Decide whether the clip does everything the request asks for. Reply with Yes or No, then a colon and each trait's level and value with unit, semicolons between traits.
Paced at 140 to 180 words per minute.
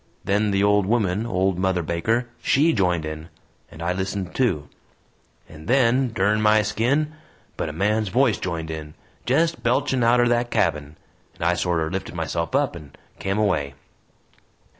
Yes: average, 160 wpm